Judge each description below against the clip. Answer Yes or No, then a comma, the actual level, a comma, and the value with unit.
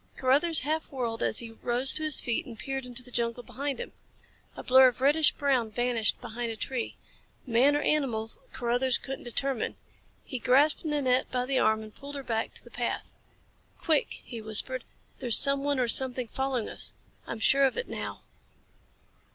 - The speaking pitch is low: No, very high, 255 Hz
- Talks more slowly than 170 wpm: No, average, 180 wpm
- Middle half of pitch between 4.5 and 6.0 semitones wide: No, average, 2.8 semitones